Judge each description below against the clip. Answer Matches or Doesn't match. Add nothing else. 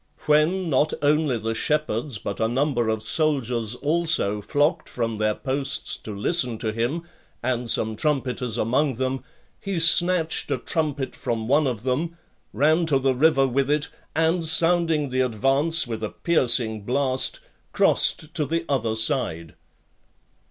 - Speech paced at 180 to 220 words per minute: Doesn't match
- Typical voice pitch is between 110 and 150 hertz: Matches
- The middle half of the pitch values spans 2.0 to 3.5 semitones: Doesn't match